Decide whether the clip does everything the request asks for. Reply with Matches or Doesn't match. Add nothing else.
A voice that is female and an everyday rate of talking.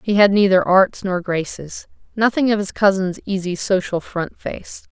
Matches